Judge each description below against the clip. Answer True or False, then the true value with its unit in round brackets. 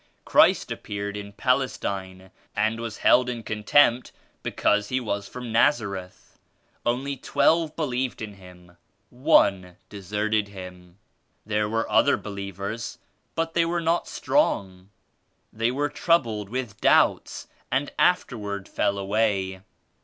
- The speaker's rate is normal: False (125 wpm)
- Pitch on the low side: True (110 Hz)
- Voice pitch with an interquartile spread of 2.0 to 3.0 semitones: False (4.3 semitones)